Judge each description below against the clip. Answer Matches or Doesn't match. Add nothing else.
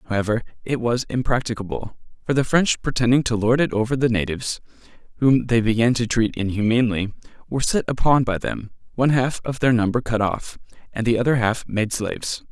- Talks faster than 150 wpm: Matches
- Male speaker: Matches